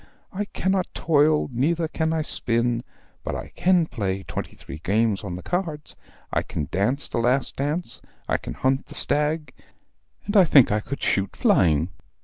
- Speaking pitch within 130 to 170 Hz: Yes, medium, 140 Hz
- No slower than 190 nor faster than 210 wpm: No, average, 170 wpm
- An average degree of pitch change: No, wide, 7.1 semitones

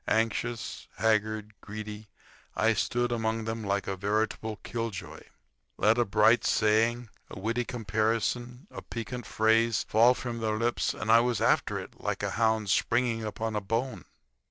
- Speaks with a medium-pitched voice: No, low, 110 Hz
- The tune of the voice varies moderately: No, narrow, 1.5 semitones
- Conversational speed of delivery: Yes, average, 155 wpm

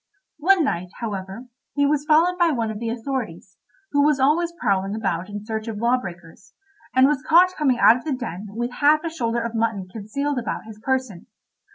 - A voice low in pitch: No, high, 235 Hz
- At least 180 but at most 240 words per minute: Yes, average, 200 wpm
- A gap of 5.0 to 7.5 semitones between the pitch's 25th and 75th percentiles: Yes, wide, 5.6 semitones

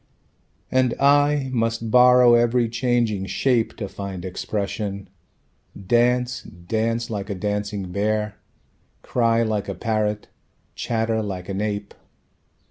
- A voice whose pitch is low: Yes, low, 110 Hz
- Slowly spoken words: Yes, slow, 115 wpm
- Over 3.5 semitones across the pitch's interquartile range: No, average, 2.9 semitones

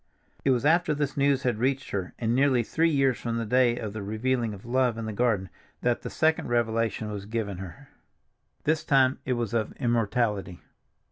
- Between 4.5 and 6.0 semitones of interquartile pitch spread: No, average, 3.3 semitones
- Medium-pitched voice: No, low, 120 Hz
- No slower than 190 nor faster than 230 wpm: Yes, average, 195 wpm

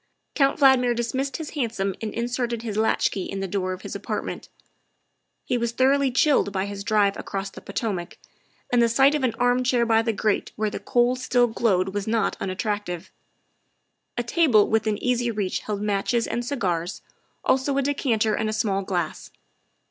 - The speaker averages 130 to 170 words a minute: No, average, 180 wpm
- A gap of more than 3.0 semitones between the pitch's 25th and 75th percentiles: Yes, average, 3.7 semitones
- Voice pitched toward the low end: No, high, 225 Hz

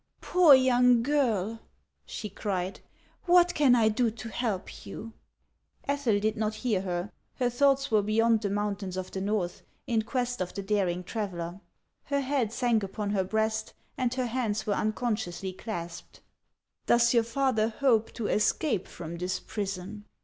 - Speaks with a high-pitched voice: Yes, high, 220 Hz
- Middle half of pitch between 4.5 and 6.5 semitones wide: No, average, 3.7 semitones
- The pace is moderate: Yes, average, 170 wpm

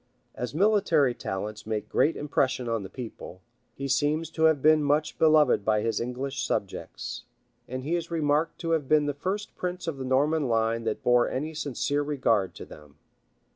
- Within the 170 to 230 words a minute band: Yes, average, 180 wpm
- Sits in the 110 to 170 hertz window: Yes, medium, 140 Hz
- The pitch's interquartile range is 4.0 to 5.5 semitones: Yes, average, 5.0 semitones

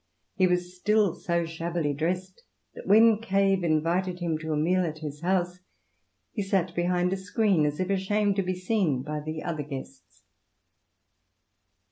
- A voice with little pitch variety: No, average, 3.2 semitones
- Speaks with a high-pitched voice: No, medium, 180 Hz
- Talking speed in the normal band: Yes, average, 160 wpm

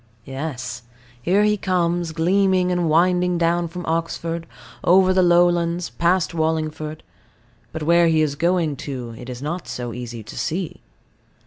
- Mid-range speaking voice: Yes, medium, 170 Hz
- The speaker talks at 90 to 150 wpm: Yes, average, 145 wpm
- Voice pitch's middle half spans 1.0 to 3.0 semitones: Yes, narrow, 2.6 semitones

